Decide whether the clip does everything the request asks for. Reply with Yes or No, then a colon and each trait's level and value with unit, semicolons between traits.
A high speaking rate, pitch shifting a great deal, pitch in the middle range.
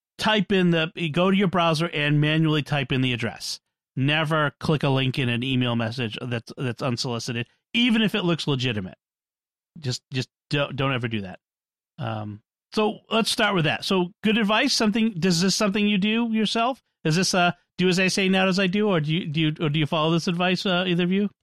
Yes: fast, 220 wpm; wide, 6.6 semitones; medium, 165 Hz